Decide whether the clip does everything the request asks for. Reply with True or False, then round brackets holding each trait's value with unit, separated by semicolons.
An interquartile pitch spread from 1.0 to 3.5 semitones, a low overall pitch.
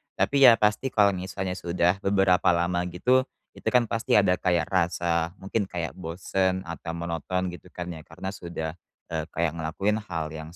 True (2.5 semitones; 90 Hz)